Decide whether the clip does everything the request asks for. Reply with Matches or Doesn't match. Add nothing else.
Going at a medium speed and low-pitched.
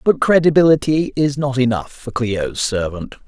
Matches